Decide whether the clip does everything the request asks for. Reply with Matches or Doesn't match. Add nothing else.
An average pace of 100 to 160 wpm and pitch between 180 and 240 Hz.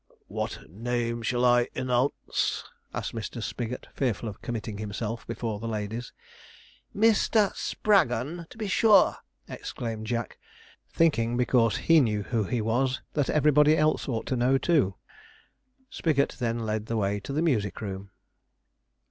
Doesn't match